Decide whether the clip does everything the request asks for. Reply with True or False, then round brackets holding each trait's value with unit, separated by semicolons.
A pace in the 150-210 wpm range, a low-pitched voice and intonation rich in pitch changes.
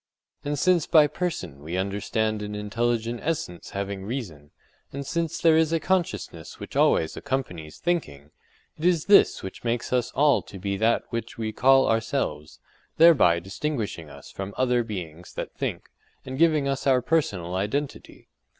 True (155 wpm; 115 Hz; 7.3 semitones)